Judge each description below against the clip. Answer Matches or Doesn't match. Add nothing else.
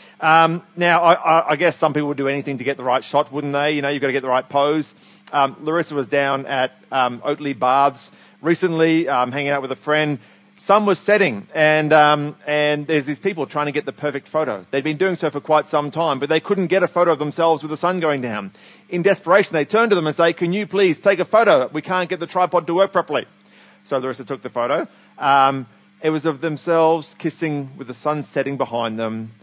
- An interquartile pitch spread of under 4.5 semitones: Matches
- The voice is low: Doesn't match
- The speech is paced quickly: Matches